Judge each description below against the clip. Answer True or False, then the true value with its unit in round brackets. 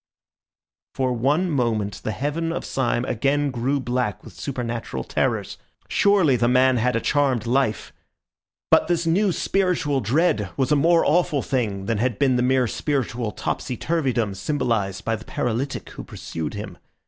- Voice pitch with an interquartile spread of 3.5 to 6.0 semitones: True (4.2 semitones)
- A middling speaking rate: True (160 wpm)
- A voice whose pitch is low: True (125 Hz)